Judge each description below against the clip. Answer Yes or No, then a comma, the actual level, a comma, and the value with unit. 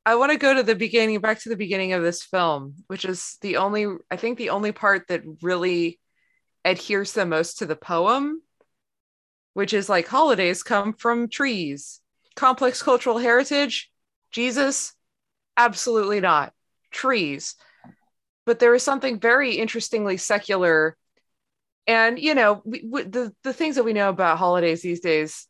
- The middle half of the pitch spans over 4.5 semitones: Yes, average, 5.0 semitones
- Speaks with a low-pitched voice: No, high, 210 Hz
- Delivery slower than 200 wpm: Yes, average, 160 wpm